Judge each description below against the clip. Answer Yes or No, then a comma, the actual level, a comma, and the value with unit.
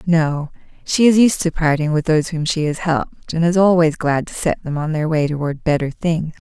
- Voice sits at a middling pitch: Yes, medium, 160 Hz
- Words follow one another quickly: Yes, fast, 230 wpm